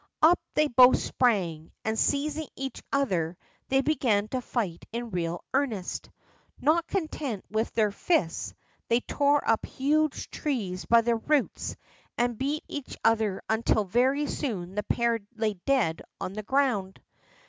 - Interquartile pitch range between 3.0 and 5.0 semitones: No, wide, 5.4 semitones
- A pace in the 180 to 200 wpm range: No, average, 150 wpm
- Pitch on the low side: No, high, 235 Hz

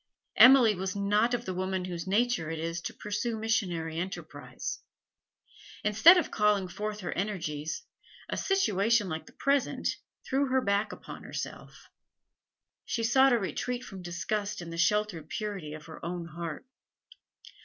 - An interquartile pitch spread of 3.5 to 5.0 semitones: Yes, average, 4.7 semitones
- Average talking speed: Yes, average, 150 wpm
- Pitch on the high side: Yes, high, 200 Hz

